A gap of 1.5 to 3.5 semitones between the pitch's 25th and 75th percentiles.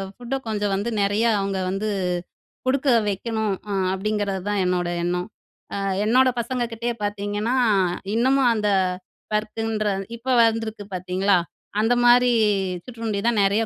Yes: average, 2.8 semitones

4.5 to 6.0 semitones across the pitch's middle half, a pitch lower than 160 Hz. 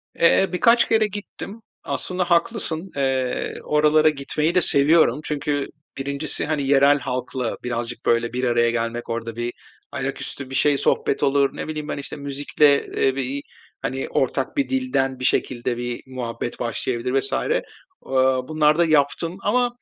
No: average, 3.6 semitones; medium, 140 Hz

